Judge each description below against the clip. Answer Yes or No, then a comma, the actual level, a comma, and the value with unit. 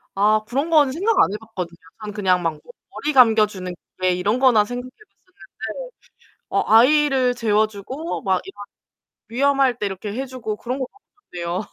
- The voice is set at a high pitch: Yes, high, 225 Hz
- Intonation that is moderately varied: Yes, average, 4.9 semitones